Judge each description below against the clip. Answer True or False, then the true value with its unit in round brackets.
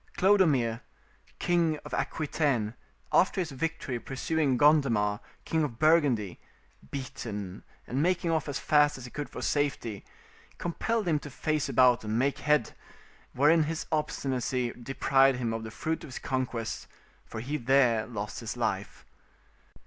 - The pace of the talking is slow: False (145 wpm)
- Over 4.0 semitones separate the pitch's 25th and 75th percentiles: True (4.5 semitones)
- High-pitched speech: False (135 Hz)